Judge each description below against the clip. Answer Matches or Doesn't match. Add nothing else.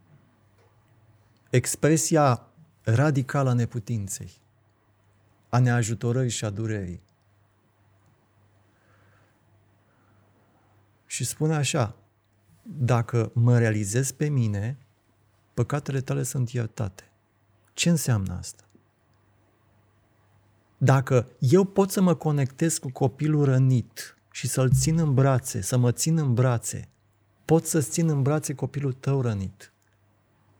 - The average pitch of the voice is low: Matches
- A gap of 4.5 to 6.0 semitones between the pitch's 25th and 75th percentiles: Doesn't match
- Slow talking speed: Matches